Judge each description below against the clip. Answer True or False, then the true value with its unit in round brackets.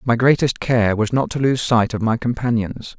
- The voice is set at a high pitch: False (120 Hz)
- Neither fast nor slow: False (220 wpm)